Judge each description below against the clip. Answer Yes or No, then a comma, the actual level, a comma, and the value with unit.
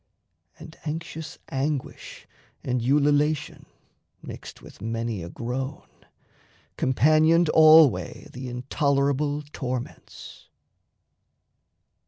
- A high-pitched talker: No, medium, 140 Hz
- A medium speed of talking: No, slow, 75 wpm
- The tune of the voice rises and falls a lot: No, average, 3.7 semitones